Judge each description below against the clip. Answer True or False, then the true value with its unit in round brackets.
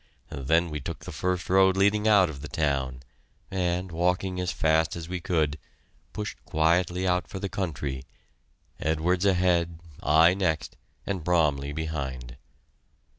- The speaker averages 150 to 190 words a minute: False (140 wpm)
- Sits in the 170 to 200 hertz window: False (85 Hz)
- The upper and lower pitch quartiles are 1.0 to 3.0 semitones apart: False (3.4 semitones)